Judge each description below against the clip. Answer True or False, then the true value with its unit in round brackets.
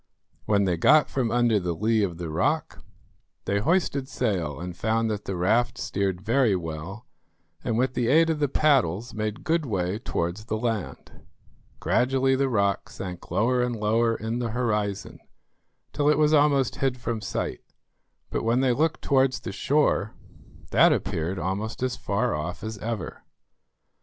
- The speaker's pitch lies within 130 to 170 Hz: False (115 Hz)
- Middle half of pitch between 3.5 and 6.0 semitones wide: True (4.6 semitones)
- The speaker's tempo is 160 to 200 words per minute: True (165 wpm)